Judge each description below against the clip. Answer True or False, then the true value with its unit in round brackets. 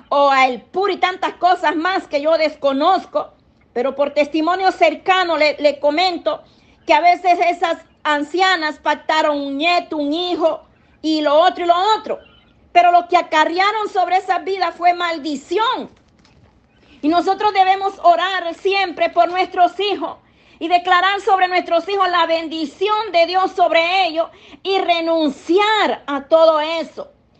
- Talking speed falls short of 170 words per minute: True (145 wpm)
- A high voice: True (345 Hz)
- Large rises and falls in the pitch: False (3.0 semitones)